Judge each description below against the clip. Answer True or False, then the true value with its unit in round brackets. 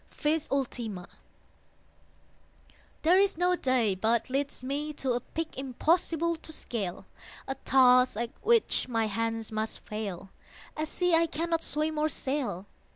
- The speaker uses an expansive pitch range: True (5.8 semitones)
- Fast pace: False (140 wpm)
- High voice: True (270 Hz)